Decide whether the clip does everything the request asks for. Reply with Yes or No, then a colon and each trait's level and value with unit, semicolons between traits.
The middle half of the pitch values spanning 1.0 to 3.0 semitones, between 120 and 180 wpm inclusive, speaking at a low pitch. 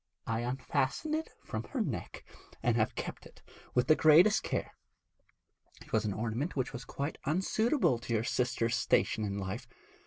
No: wide, 5.5 semitones; average, 165 wpm; low, 125 Hz